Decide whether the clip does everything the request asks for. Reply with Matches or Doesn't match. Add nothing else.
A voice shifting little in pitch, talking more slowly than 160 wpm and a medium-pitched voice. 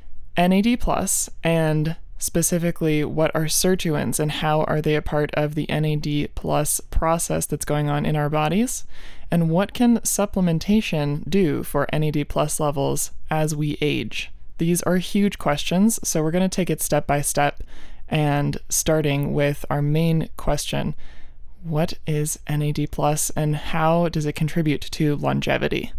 Matches